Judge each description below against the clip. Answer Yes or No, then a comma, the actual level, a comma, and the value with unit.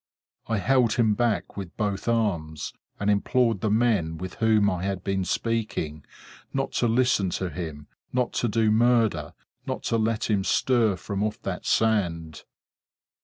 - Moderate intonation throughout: Yes, average, 3.7 semitones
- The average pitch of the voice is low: Yes, low, 105 Hz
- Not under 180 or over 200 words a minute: No, average, 160 wpm